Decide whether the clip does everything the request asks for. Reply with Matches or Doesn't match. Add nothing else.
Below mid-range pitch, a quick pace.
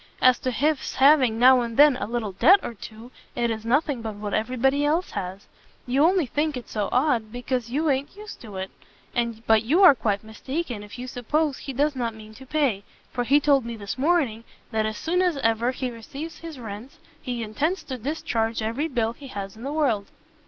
Doesn't match